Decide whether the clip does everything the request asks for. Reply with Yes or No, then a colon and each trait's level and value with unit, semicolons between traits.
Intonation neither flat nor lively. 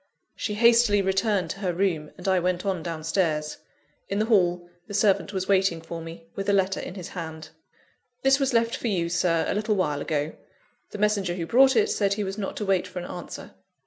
Yes: average, 3.5 semitones